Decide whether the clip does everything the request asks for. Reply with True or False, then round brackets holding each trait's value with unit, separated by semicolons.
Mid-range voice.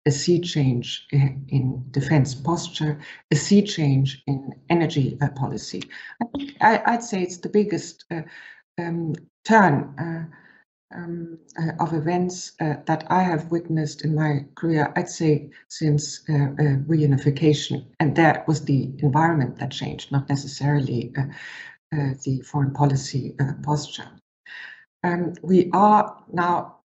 True (155 Hz)